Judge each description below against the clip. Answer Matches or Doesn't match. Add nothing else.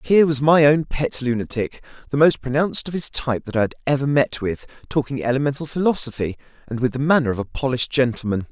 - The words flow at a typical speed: Matches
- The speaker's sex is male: Matches